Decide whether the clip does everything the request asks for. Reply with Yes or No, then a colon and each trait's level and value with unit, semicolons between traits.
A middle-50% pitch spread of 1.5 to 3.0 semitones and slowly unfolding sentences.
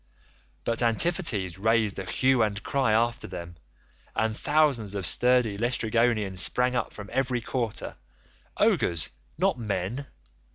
No: average, 3.6 semitones; slow, 120 wpm